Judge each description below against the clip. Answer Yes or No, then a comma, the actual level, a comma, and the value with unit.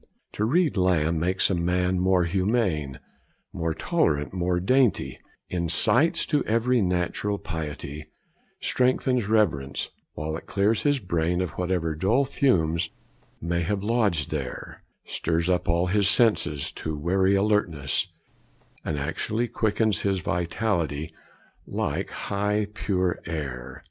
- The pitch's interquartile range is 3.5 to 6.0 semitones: Yes, average, 4.4 semitones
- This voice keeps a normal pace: No, slow, 125 wpm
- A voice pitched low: Yes, very low, 90 Hz